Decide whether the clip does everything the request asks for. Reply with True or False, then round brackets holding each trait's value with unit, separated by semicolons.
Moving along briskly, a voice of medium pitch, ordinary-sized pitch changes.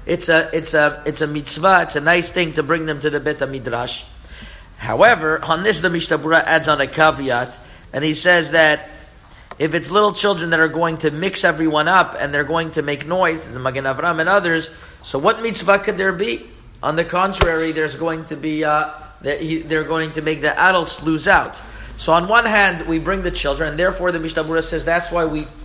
False (215 wpm; 160 Hz; 2.2 semitones)